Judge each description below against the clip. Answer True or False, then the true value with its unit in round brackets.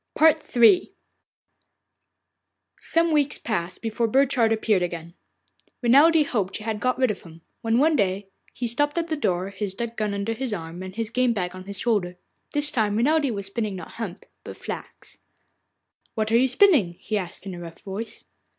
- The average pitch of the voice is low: False (225 Hz)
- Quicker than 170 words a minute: True (180 wpm)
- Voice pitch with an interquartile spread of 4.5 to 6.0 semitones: True (5.2 semitones)